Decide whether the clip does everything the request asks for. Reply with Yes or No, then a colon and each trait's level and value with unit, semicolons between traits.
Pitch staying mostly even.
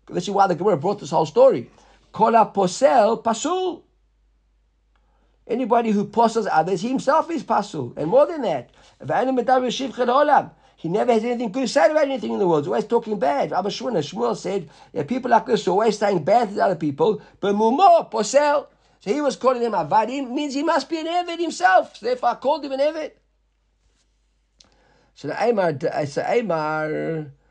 No: wide, 5.5 semitones